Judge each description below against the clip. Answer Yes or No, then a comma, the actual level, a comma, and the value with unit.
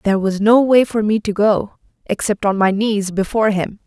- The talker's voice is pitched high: Yes, high, 205 Hz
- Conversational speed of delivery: No, fast, 215 wpm